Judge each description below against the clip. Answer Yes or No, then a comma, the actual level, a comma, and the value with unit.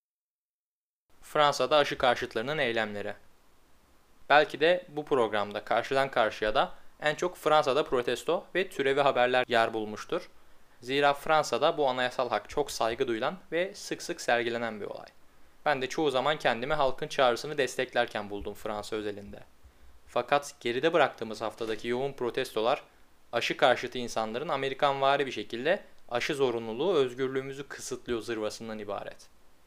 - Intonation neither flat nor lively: Yes, average, 4.8 semitones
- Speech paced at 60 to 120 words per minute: No, average, 130 wpm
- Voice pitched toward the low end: Yes, low, 120 Hz